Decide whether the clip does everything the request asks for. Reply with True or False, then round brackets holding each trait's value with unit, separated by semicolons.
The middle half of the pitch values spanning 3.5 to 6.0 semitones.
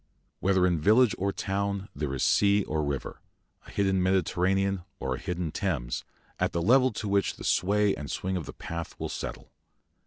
False (3.1 semitones)